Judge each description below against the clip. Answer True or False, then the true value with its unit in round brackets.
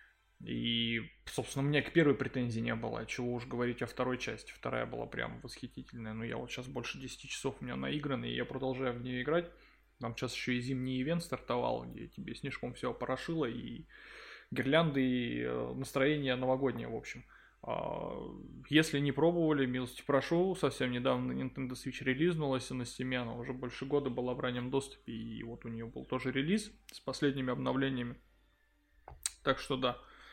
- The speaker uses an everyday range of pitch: False (2.3 semitones)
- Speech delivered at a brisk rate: True (175 wpm)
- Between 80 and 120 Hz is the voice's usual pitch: False (130 Hz)